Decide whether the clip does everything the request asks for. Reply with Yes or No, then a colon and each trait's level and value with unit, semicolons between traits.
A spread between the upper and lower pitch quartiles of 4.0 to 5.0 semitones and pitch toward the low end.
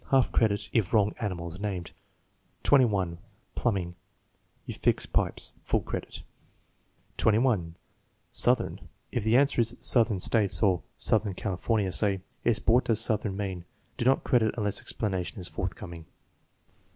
No: average, 3.6 semitones; low, 105 Hz